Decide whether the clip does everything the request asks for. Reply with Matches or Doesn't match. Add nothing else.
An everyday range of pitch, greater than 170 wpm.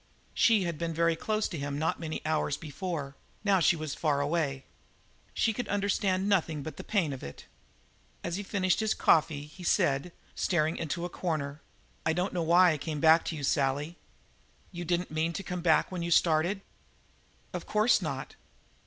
Matches